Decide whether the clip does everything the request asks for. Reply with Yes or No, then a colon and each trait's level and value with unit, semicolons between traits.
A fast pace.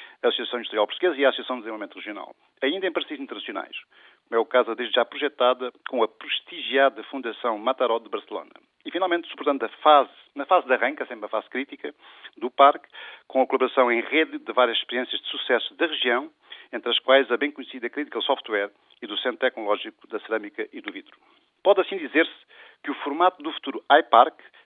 Yes: fast, 195 wpm